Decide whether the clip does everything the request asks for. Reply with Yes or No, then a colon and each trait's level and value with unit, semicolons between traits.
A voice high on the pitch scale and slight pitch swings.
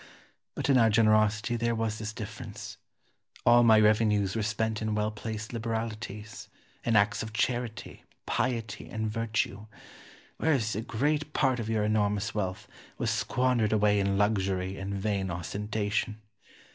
No: low, 110 Hz; narrow, 1.7 semitones